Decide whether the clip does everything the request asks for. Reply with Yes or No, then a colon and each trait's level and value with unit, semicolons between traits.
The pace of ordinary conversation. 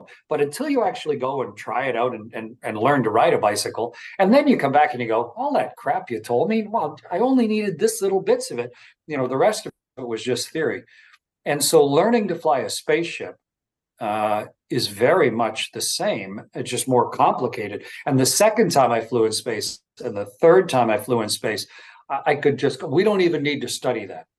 No: fast, 230 wpm